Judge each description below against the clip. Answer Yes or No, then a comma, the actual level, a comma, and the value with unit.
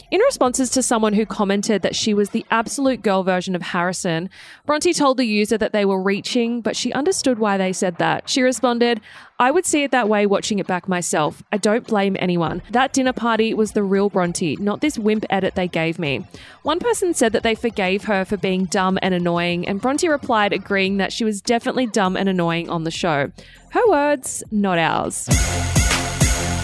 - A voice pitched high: Yes, high, 210 Hz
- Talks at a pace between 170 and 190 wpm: No, fast, 205 wpm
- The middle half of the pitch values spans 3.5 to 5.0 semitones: Yes, average, 4.6 semitones